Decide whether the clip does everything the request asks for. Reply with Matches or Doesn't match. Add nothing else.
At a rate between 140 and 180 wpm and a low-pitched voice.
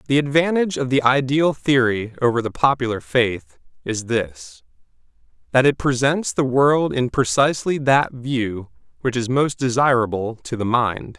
Matches